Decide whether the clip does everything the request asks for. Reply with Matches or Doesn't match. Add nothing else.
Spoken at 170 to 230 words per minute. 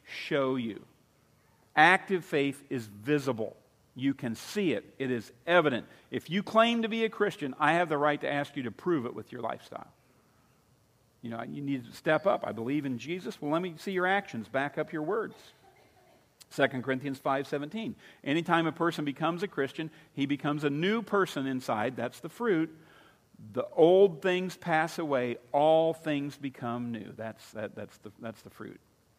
Matches